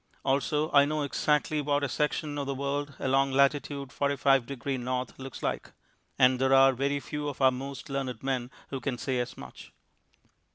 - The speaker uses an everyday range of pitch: No, narrow, 1.4 semitones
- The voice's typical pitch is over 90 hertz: Yes, medium, 140 Hz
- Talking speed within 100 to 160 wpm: No, average, 180 wpm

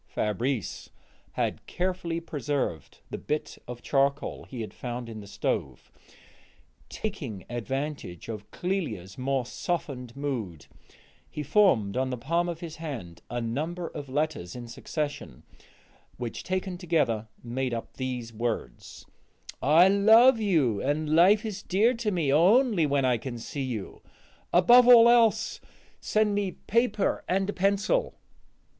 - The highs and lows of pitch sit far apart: Yes, wide, 7.6 semitones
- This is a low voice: No, medium, 145 Hz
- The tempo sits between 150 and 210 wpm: No, average, 140 wpm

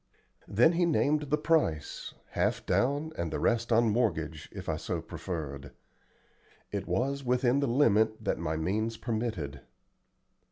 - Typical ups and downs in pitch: No, wide, 8.5 semitones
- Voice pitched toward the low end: Yes, low, 115 Hz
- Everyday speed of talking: Yes, average, 145 wpm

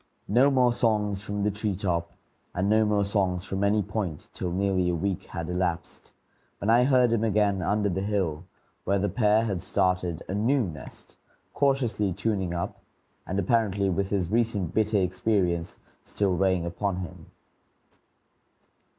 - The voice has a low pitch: Yes, low, 100 Hz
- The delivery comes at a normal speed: Yes, average, 160 wpm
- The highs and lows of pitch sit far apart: No, average, 2.8 semitones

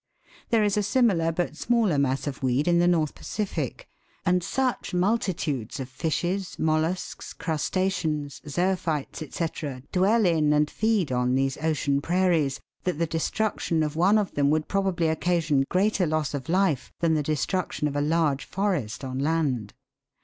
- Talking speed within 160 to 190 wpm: Yes, average, 165 wpm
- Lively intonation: No, average, 4.3 semitones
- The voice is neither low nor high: Yes, medium, 160 Hz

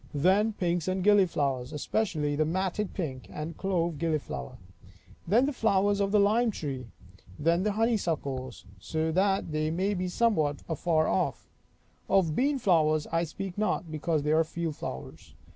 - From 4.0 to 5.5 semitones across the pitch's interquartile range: Yes, average, 4.6 semitones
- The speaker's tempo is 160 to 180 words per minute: No, average, 145 wpm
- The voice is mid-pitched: Yes, medium, 170 Hz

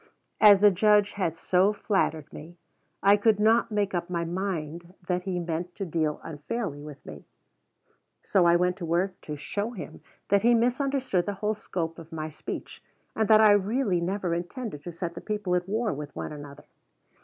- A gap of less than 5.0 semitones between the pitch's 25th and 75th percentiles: Yes, average, 3.8 semitones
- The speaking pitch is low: No, medium, 180 Hz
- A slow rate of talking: No, average, 190 wpm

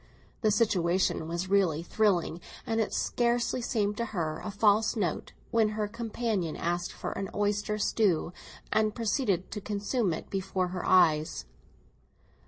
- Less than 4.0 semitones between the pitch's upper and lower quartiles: Yes, average, 3.5 semitones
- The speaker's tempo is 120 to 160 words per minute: Yes, average, 145 wpm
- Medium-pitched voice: No, high, 205 Hz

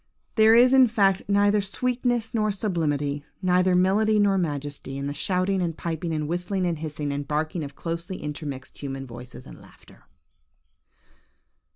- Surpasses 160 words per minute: No, average, 155 wpm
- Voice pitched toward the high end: No, medium, 175 Hz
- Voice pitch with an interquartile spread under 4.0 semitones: No, wide, 5.6 semitones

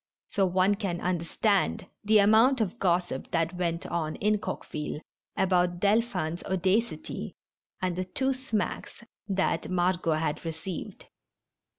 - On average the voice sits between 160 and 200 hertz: Yes, medium, 185 Hz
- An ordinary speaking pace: No, slow, 120 wpm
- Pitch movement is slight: No, average, 3.3 semitones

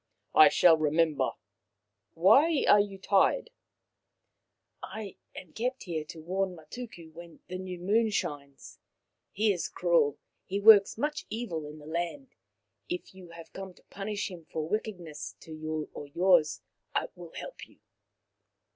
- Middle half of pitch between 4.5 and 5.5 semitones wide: Yes, average, 4.8 semitones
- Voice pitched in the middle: Yes, medium, 180 Hz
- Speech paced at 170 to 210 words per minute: No, average, 155 wpm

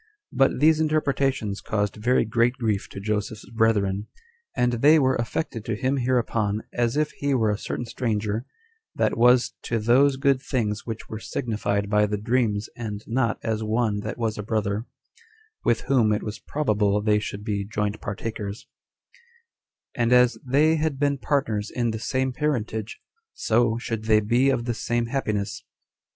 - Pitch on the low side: Yes, low, 115 Hz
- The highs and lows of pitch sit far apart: No, average, 3.4 semitones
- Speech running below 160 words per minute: No, average, 165 wpm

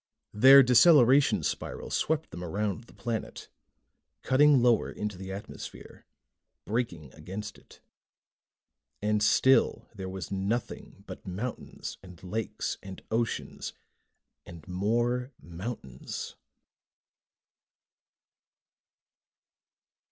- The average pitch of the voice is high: No, low, 105 Hz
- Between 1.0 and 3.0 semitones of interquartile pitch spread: No, average, 4.6 semitones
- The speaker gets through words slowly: Yes, slow, 90 wpm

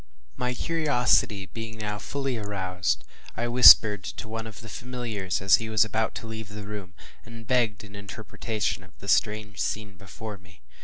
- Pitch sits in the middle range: No, low, 110 Hz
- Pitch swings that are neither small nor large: No, narrow, 2.3 semitones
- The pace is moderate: Yes, average, 170 wpm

